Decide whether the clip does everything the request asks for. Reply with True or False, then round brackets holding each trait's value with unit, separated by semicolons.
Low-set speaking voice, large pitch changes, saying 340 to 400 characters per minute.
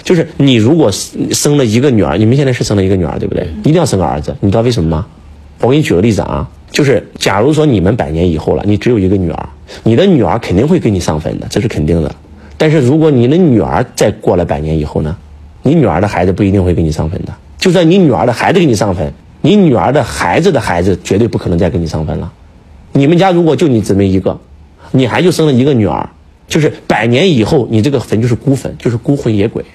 True (105 Hz; 7.6 semitones; 375 characters per minute)